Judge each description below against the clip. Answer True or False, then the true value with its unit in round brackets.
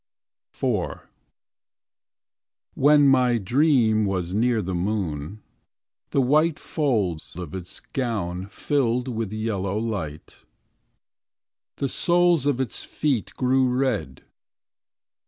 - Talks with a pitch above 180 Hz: False (115 Hz)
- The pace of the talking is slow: True (100 wpm)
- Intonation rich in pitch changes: True (5.9 semitones)